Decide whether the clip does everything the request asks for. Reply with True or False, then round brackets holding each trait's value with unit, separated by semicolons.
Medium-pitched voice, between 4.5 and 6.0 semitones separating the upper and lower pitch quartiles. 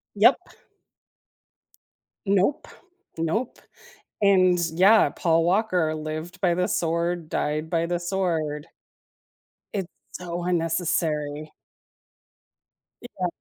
False (175 Hz; 2.5 semitones)